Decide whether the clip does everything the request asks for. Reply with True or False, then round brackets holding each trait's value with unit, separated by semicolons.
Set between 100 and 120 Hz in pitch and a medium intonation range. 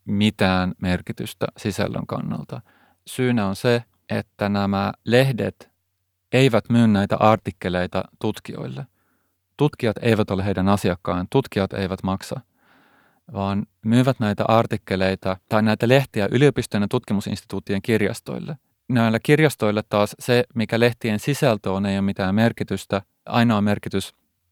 True (105 Hz; 3.3 semitones)